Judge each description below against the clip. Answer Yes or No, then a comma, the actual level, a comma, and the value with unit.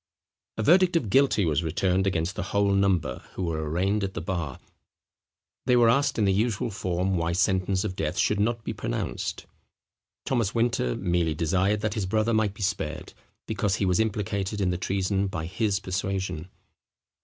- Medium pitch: No, very low, 95 Hz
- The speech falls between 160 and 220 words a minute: Yes, average, 180 wpm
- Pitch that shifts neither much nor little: Yes, average, 3.2 semitones